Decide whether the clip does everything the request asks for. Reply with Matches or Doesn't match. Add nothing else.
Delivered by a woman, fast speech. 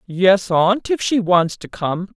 Doesn't match